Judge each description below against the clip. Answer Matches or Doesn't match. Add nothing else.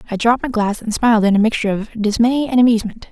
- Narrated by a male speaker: Doesn't match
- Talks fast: Matches